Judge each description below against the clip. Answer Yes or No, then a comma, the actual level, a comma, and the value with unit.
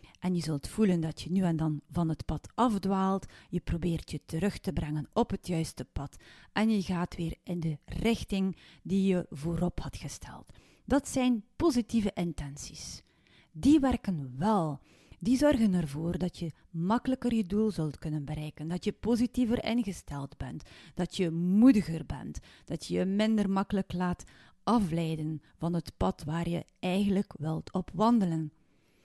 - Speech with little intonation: No, average, 4.8 semitones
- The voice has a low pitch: No, medium, 180 Hz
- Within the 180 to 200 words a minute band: No, average, 160 wpm